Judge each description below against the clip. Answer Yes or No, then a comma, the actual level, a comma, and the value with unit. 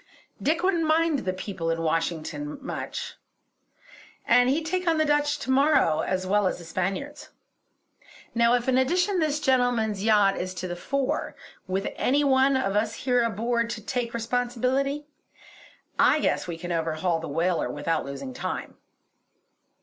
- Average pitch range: No, wide, 7.3 semitones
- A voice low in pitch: No, high, 240 Hz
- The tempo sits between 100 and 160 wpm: Yes, average, 155 wpm